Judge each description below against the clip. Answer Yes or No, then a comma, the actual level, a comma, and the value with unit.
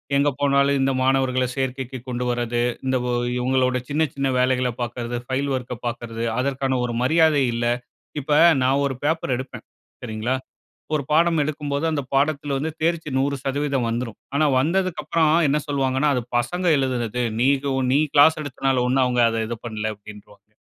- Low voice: Yes, low, 130 Hz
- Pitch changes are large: No, narrow, 2.5 semitones